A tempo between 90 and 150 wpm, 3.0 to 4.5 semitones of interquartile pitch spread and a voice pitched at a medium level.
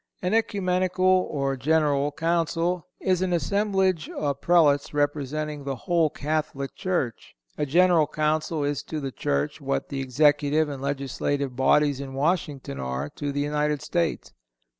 Yes: average, 140 wpm; average, 3.4 semitones; medium, 150 Hz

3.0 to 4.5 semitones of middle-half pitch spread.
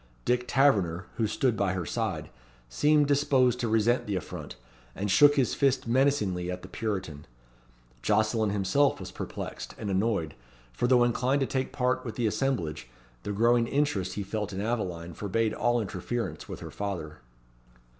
No: average, 5.1 semitones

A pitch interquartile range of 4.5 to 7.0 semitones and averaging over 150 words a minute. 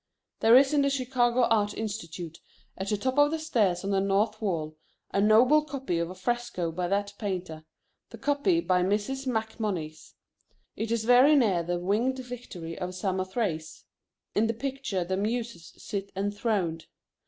Yes: average, 5.2 semitones; average, 165 wpm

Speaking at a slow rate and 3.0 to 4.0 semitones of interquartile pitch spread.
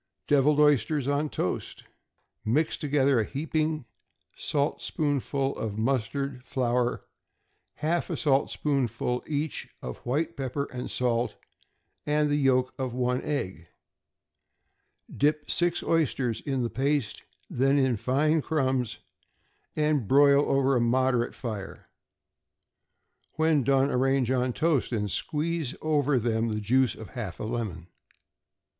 Yes: slow, 120 wpm; average, 3.3 semitones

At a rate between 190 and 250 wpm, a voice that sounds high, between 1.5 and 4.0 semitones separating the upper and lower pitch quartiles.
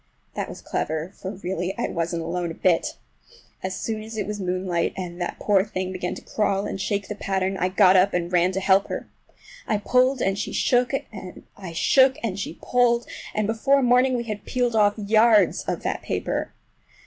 Yes: average, 195 wpm; high, 195 Hz; average, 3.3 semitones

